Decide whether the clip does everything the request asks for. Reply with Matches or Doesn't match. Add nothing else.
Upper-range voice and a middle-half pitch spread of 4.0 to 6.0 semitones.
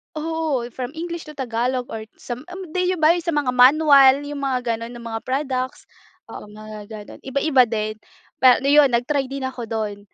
Matches